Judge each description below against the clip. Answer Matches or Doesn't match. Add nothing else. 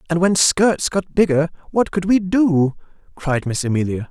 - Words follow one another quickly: Doesn't match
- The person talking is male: Matches